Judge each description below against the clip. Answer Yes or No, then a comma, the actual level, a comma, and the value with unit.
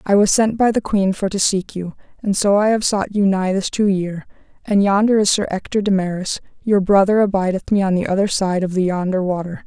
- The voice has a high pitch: Yes, high, 195 Hz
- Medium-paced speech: No, fast, 240 wpm